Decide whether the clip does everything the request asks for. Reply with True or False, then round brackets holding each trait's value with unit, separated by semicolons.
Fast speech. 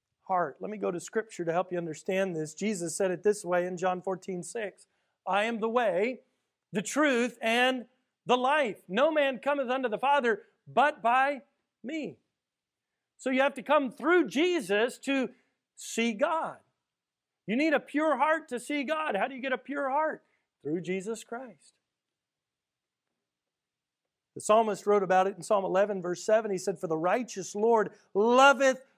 False (170 wpm)